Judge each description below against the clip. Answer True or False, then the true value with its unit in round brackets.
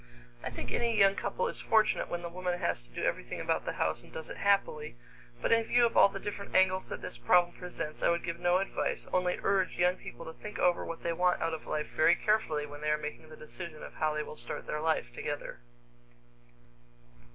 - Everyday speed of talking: False (230 wpm)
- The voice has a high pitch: False (175 Hz)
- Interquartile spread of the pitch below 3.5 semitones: False (4.0 semitones)